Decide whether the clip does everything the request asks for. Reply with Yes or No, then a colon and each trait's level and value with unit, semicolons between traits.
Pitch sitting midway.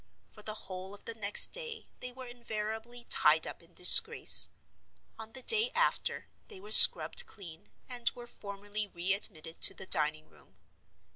No: high, 215 Hz